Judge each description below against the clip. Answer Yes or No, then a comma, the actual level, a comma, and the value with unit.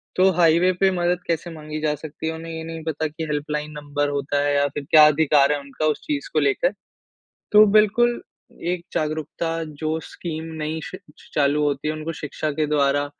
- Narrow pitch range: Yes, narrow, 2.3 semitones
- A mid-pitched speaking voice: Yes, medium, 155 Hz